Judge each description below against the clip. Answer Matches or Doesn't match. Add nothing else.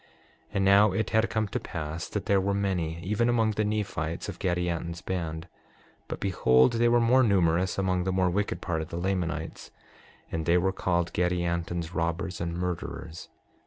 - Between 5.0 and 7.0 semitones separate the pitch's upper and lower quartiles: Doesn't match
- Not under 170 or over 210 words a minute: Matches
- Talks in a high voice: Doesn't match